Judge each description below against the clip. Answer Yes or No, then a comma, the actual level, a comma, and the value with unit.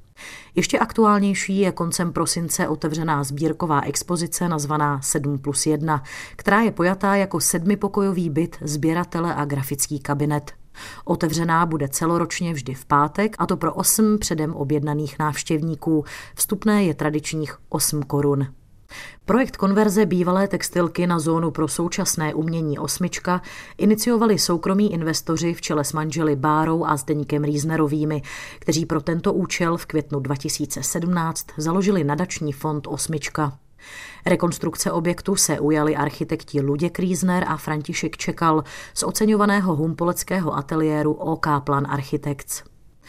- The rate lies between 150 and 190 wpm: No, average, 125 wpm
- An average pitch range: Yes, average, 3.0 semitones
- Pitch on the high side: No, medium, 160 Hz